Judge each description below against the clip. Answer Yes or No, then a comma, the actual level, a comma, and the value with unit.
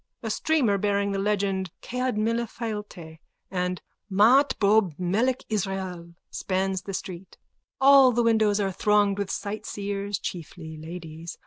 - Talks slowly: Yes, slow, 130 wpm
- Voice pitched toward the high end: Yes, high, 200 Hz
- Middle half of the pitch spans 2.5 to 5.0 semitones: Yes, average, 3.1 semitones